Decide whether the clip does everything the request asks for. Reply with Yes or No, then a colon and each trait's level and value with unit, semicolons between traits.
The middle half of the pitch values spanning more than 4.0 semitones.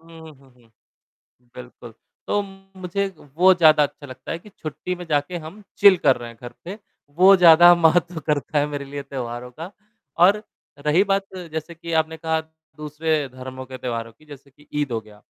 Yes: average, 4.9 semitones